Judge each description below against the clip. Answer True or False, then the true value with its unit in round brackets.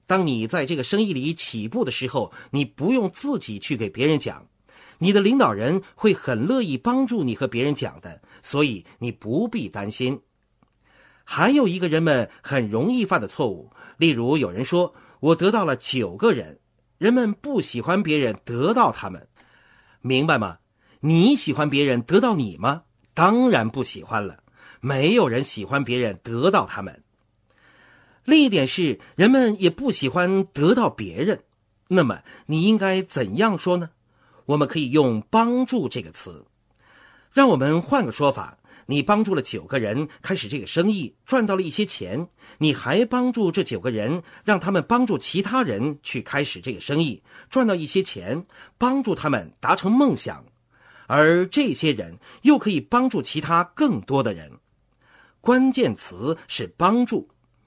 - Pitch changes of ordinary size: False (8.2 semitones)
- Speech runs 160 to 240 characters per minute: True (235 characters per minute)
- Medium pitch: True (165 Hz)